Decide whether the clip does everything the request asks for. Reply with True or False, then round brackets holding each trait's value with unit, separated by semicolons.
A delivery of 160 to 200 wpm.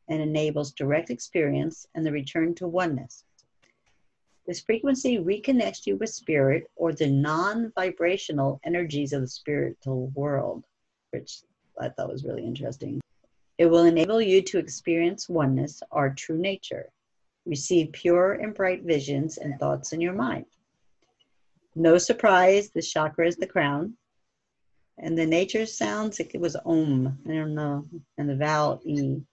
False (145 wpm)